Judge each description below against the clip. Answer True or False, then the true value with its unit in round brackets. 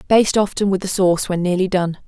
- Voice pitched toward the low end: False (185 Hz)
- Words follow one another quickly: True (230 wpm)